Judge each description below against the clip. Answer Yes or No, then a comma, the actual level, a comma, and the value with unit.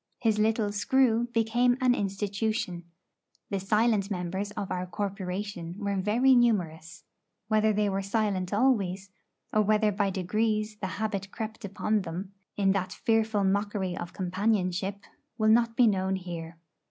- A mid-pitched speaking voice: No, high, 205 Hz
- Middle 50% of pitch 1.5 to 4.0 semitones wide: Yes, narrow, 2.5 semitones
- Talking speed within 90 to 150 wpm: Yes, average, 140 wpm